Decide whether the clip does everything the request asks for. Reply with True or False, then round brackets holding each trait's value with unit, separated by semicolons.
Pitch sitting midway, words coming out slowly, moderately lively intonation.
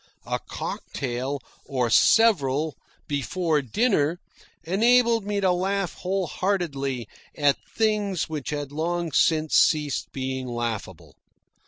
False (155 Hz; 110 wpm; 6.1 semitones)